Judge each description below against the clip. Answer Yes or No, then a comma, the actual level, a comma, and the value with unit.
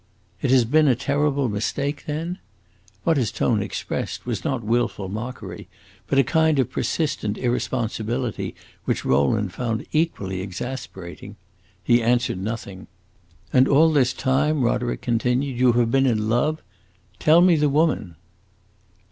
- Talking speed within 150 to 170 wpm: No, average, 140 wpm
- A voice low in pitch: Yes, low, 125 Hz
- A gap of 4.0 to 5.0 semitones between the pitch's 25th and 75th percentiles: Yes, average, 4.6 semitones